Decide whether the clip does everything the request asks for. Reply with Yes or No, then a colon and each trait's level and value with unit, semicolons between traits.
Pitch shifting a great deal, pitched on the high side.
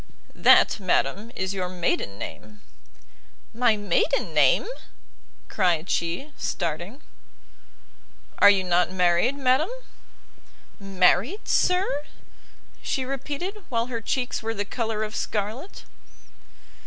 Yes: wide, 6.0 semitones; high, 210 Hz